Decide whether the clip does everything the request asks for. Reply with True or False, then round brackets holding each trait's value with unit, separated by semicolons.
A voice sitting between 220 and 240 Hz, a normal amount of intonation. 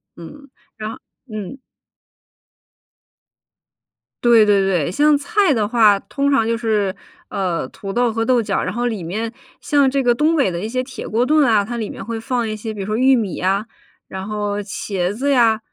True (225 Hz; 3.9 semitones)